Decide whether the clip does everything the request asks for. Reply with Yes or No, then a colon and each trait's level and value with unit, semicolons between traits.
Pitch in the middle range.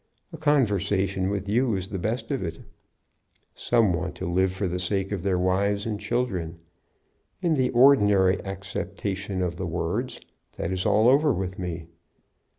No: very low, 95 Hz